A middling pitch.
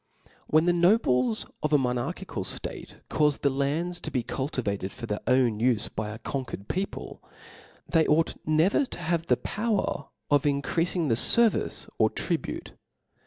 Yes: medium, 145 Hz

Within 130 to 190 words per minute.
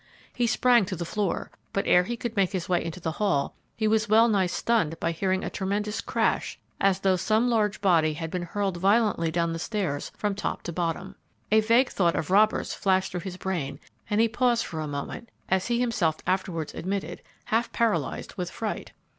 No: fast, 205 wpm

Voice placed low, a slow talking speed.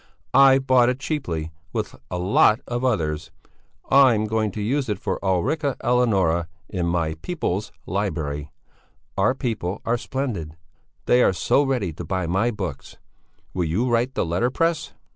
No: low, 105 Hz; average, 150 wpm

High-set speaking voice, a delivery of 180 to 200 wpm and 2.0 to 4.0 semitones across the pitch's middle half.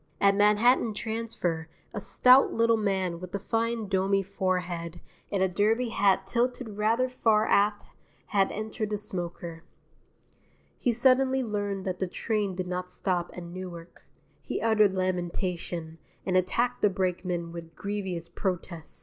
No: high, 195 Hz; average, 140 wpm; average, 3.4 semitones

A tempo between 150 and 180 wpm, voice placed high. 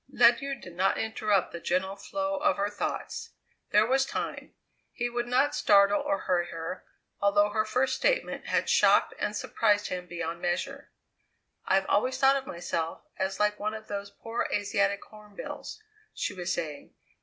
Yes: average, 165 wpm; high, 205 Hz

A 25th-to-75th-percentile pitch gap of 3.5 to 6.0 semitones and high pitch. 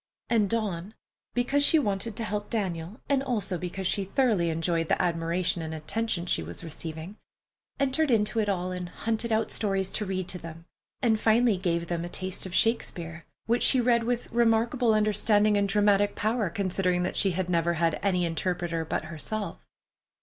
Yes: average, 4.4 semitones; high, 195 Hz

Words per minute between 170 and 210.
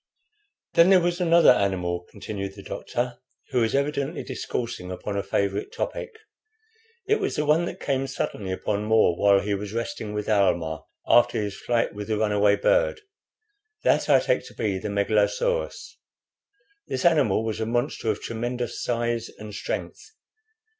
No: average, 160 wpm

